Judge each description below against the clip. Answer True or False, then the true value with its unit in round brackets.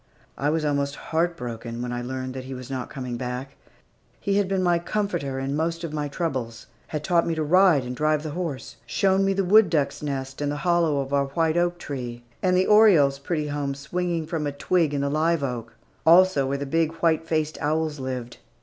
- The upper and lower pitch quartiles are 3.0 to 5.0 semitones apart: True (4.0 semitones)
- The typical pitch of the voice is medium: True (150 Hz)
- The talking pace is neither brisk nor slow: False (220 wpm)